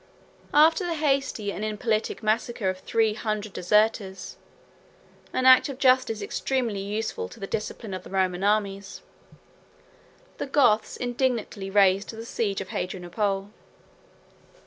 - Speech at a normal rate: No, slow, 125 wpm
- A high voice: Yes, high, 215 Hz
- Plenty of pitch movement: No, average, 3.7 semitones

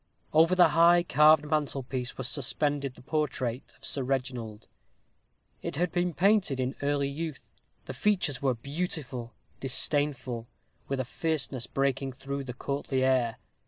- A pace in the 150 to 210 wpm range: No, average, 140 wpm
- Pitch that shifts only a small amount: No, average, 3.1 semitones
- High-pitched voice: No, medium, 140 Hz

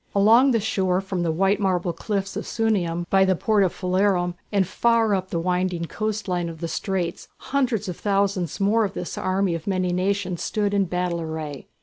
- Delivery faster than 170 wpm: Yes, average, 200 wpm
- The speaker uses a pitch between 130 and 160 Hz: No, high, 190 Hz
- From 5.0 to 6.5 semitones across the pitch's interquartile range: No, narrow, 2.4 semitones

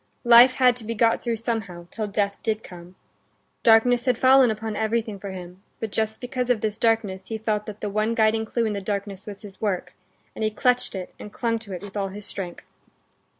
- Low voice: No, high, 215 Hz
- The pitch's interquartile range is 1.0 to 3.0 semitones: Yes, narrow, 2.5 semitones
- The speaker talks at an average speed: No, fast, 220 wpm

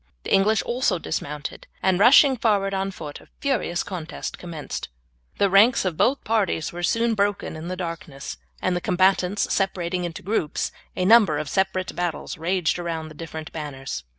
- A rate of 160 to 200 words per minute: Yes, average, 170 wpm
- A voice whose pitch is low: No, medium, 180 Hz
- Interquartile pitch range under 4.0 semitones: Yes, average, 3.5 semitones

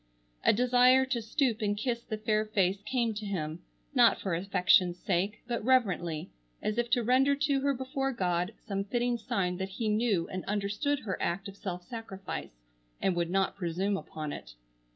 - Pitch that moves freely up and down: No, average, 4.9 semitones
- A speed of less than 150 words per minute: No, average, 180 wpm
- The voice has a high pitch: Yes, high, 205 Hz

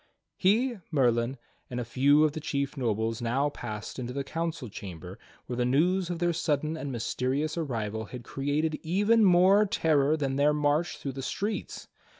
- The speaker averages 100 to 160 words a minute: No, average, 170 wpm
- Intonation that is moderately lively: Yes, average, 4.8 semitones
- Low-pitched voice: No, medium, 145 Hz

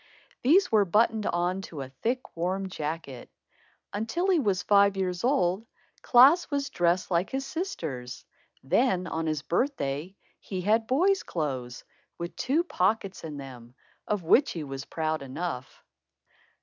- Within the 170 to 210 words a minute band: No, average, 145 wpm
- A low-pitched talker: No, medium, 185 Hz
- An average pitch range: No, wide, 7.0 semitones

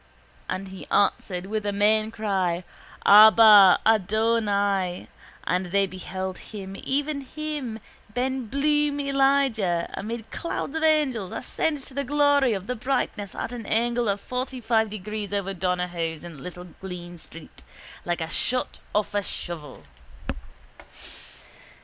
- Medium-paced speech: No, slow, 130 wpm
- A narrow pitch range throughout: No, average, 5.2 semitones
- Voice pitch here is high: Yes, high, 210 Hz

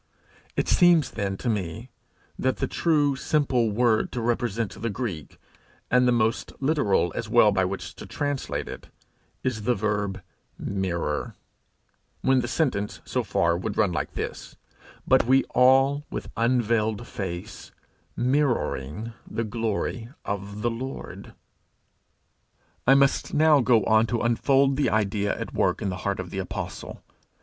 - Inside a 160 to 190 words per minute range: No, average, 145 wpm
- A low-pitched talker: Yes, low, 115 Hz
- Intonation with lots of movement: No, average, 4.4 semitones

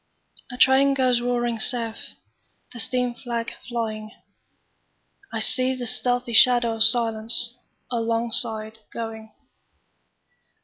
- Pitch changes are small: Yes, narrow, 1.7 semitones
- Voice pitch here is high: Yes, high, 235 Hz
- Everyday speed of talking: No, slow, 85 wpm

